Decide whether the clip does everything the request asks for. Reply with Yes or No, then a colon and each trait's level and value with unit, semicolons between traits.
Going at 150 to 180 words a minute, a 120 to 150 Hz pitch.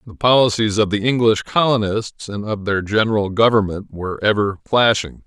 No: average, 160 wpm; low, 105 Hz